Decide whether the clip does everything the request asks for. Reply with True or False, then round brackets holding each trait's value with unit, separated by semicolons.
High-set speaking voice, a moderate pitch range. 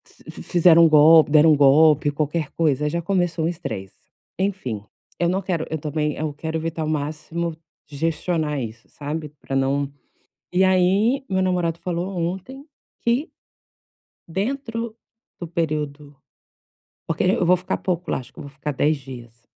False (160 Hz; 3.4 semitones)